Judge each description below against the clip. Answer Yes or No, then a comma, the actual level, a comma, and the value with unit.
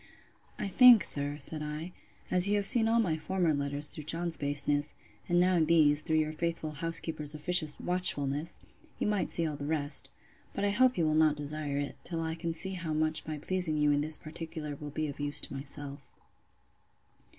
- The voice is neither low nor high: Yes, medium, 155 Hz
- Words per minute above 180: Yes, average, 195 wpm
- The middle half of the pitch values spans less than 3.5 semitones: Yes, average, 2.9 semitones